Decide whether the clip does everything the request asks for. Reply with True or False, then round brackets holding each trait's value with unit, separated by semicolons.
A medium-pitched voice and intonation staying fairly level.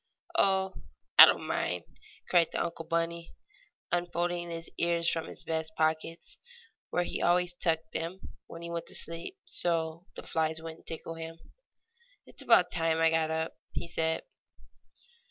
True (165 Hz; 1.1 semitones)